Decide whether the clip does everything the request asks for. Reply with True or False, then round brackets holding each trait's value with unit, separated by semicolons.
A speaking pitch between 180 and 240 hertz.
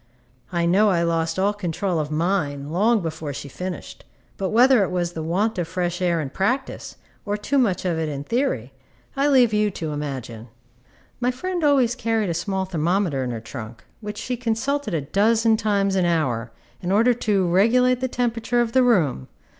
True (190 Hz)